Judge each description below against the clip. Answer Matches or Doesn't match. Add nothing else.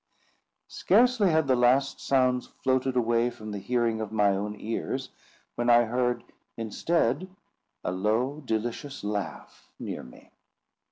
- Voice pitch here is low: Matches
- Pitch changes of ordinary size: Matches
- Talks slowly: Matches